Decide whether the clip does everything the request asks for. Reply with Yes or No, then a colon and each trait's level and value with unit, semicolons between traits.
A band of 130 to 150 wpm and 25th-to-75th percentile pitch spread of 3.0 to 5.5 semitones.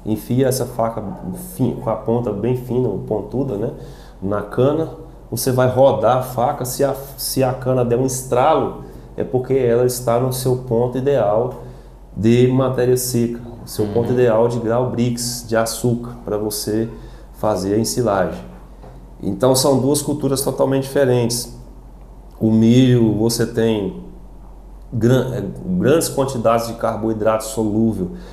No: average, 140 wpm; narrow, 2.6 semitones